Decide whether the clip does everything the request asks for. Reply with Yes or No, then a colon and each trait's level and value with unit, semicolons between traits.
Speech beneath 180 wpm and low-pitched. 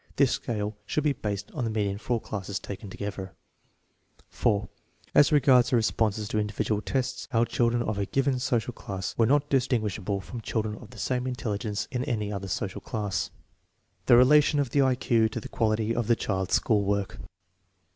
No: average, 185 wpm; low, 110 Hz